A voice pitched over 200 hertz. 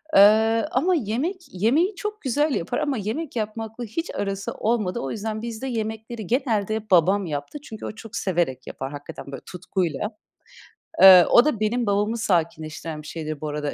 Yes: high, 215 Hz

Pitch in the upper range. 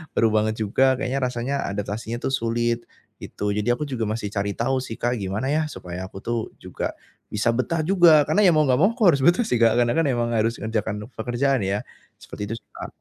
No: low, 120 Hz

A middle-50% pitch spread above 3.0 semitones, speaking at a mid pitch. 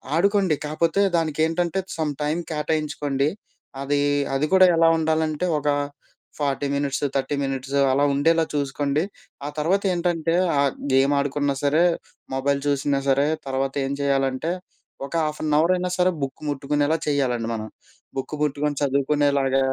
No: narrow, 2.5 semitones; medium, 145 Hz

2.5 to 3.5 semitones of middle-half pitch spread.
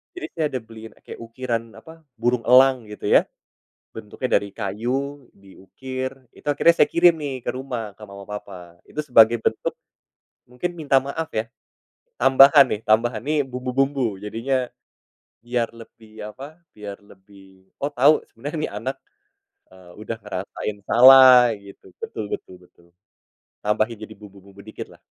No: average, 4.3 semitones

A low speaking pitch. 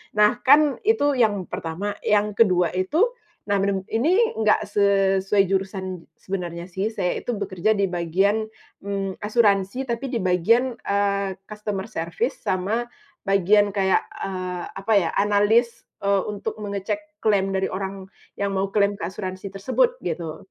No: high, 200 Hz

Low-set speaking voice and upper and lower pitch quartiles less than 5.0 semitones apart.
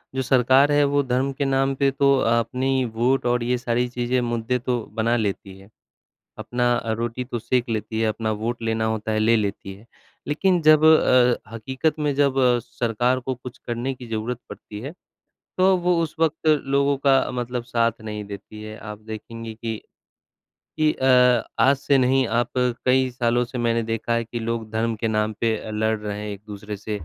Yes: low, 120 Hz; average, 3.0 semitones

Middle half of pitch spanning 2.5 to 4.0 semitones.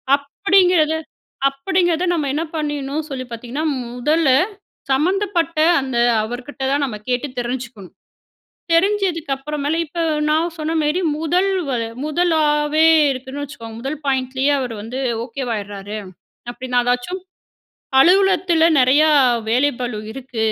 No: average, 4.6 semitones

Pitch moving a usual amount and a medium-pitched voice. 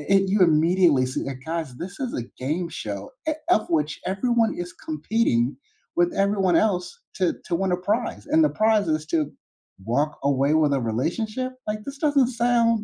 No: wide, 6.4 semitones; medium, 180 Hz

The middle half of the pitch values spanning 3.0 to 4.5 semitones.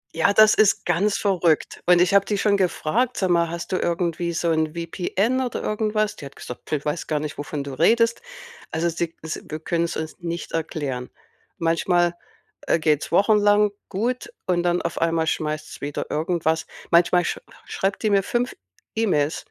Yes: average, 4.1 semitones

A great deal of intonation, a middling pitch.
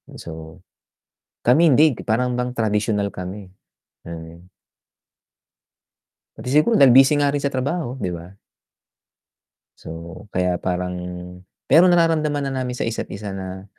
No: wide, 7.4 semitones; low, 115 Hz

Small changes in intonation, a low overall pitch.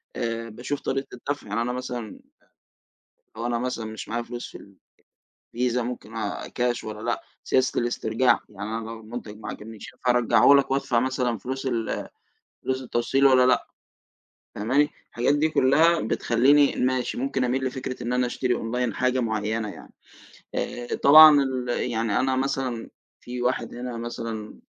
Yes: narrow, 2.2 semitones; low, 125 Hz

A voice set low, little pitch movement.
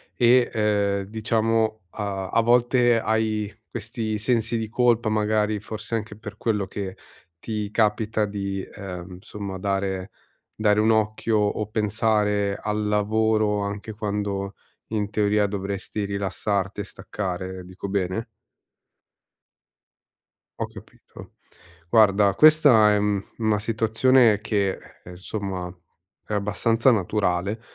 Yes: low, 105 Hz; narrow, 1.8 semitones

